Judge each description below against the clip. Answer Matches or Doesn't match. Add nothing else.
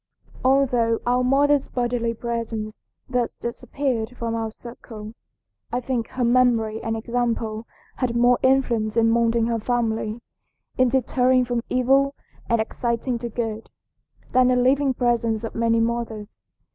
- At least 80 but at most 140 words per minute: Matches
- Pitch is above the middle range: Matches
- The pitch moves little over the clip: Matches